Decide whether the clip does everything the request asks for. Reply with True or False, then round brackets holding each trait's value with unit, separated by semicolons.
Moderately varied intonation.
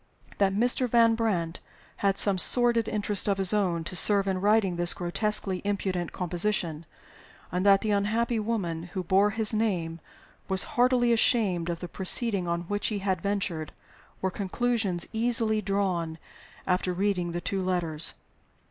True (3.4 semitones)